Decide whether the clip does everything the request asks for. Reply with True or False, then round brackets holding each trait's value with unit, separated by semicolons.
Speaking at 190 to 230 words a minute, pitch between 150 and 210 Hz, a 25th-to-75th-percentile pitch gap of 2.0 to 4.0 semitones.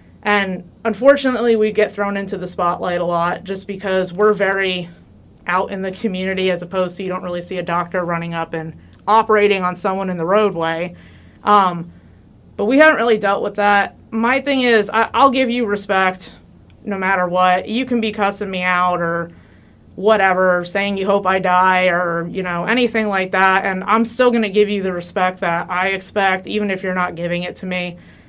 True (200 wpm; 190 Hz; 2.8 semitones)